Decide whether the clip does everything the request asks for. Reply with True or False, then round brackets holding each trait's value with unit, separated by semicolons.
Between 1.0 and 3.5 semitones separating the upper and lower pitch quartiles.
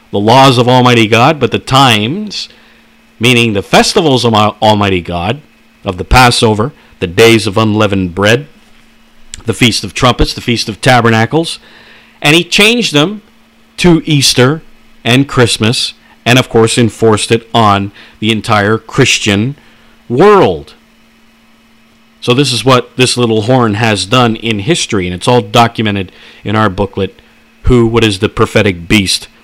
True (2.9 semitones)